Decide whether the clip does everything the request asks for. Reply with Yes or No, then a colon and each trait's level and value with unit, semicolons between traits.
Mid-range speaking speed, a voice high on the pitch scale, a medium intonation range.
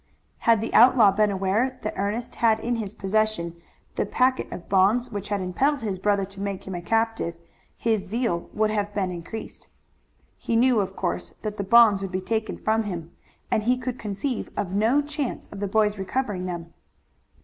Yes: average, 190 wpm; high, 210 Hz; average, 3.0 semitones